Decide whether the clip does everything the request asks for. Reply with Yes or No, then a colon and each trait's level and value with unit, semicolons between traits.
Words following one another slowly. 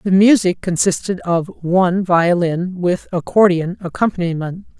Yes: slow, 115 wpm